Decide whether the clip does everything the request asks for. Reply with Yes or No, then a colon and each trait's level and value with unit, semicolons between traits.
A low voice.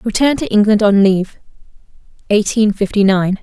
No: high, 210 Hz